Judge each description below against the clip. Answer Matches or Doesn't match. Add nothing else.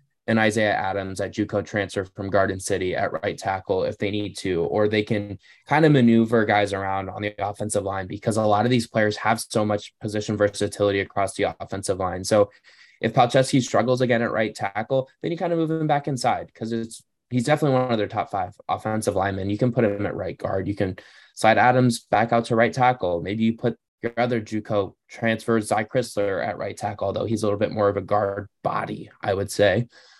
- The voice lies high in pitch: Doesn't match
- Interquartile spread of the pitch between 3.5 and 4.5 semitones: Doesn't match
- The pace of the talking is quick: Matches